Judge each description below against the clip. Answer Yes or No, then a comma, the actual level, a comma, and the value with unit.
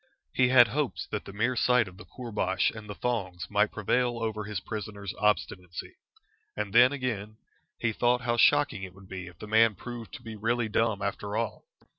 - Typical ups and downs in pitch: Yes, average, 3.1 semitones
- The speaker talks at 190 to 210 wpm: Yes, average, 195 wpm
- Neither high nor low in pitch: No, low, 110 Hz